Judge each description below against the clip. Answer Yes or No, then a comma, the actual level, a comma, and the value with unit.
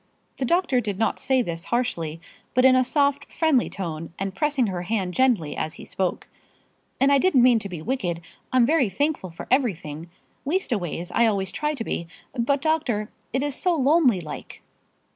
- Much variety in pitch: Yes, wide, 7.1 semitones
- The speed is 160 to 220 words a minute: Yes, average, 180 wpm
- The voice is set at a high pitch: Yes, high, 240 Hz